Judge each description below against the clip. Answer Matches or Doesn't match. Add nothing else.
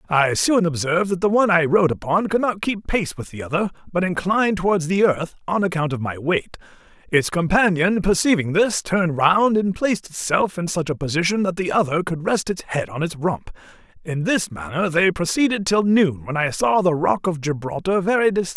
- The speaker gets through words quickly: Matches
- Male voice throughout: Matches